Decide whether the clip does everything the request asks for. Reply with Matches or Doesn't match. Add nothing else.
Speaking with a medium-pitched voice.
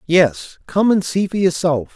Matches